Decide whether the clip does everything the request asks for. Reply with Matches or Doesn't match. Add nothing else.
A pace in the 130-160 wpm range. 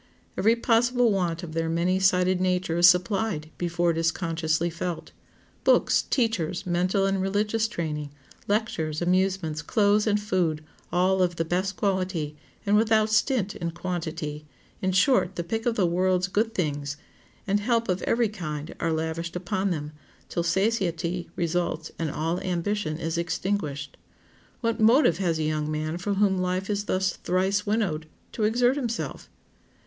Matches